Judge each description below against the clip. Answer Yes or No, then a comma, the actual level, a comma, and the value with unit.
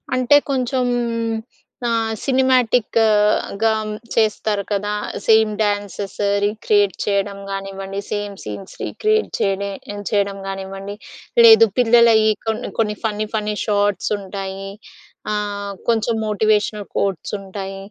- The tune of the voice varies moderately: No, narrow, 2.0 semitones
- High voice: Yes, high, 210 Hz